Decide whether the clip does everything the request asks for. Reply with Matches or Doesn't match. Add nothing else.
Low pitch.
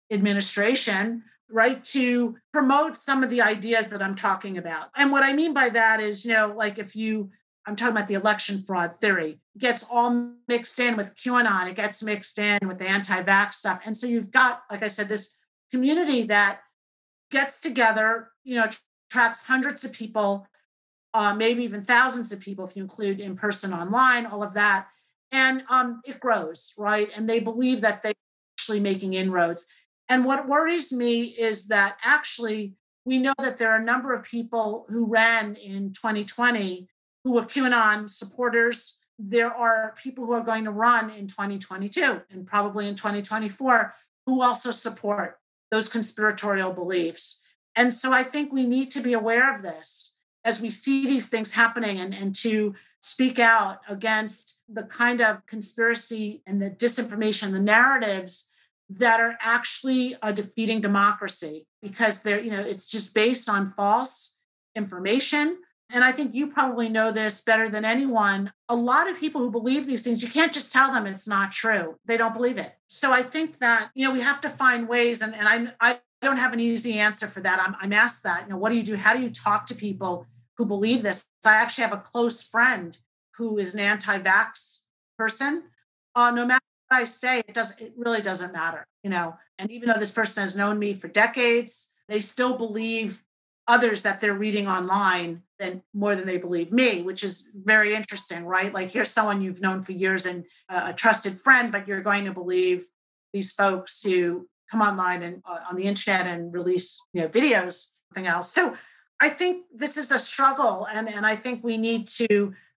Doesn't match